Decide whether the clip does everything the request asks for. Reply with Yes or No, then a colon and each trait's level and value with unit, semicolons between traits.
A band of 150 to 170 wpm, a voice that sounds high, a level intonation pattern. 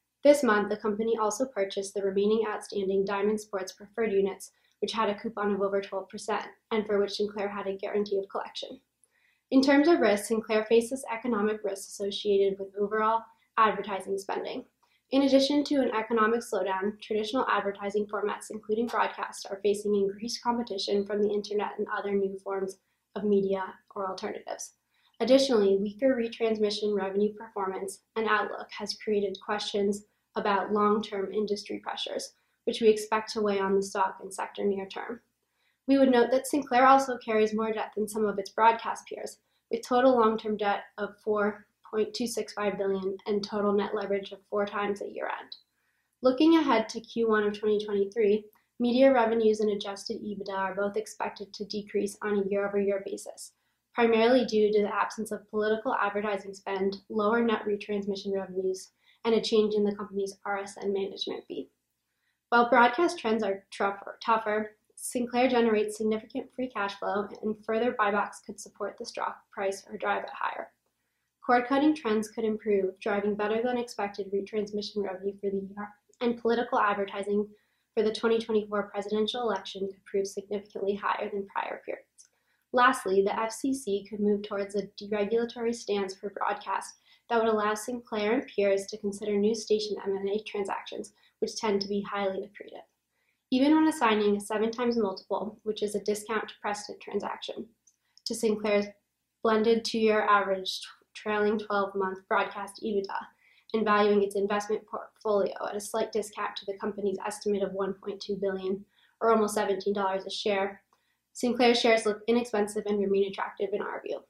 Yes: average, 160 wpm; high, 210 Hz; narrow, 1.9 semitones